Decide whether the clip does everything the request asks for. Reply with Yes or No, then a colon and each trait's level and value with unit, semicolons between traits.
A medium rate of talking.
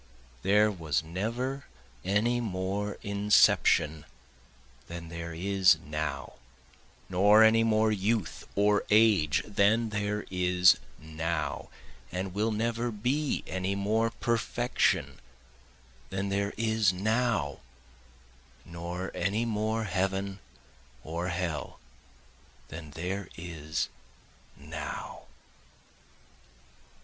No: slow, 90 wpm